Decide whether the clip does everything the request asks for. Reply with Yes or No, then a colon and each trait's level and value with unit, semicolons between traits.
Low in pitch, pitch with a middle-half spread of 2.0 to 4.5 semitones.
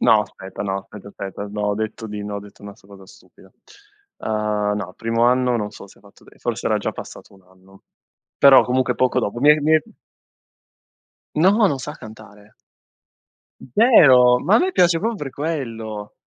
No: low, 110 Hz; wide, 5.4 semitones